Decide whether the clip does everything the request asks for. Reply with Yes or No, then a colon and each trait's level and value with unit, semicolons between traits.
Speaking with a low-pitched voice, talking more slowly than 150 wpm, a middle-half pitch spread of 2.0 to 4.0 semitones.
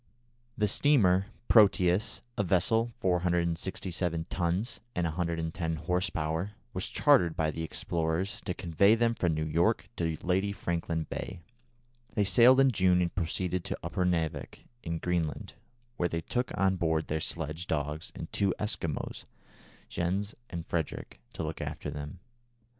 Yes: very low, 90 Hz; average, 140 wpm; average, 2.9 semitones